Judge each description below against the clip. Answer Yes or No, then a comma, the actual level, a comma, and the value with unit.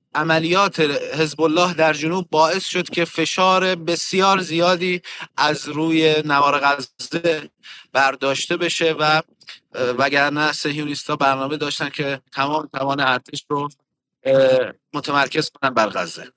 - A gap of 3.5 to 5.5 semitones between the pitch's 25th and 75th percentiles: No, average, 2.8 semitones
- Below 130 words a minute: Yes, average, 115 wpm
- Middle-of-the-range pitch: Yes, medium, 155 Hz